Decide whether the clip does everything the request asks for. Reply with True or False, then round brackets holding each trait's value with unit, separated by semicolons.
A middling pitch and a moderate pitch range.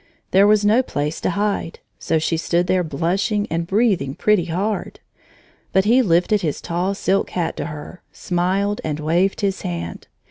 True (180 Hz; 3.7 semitones)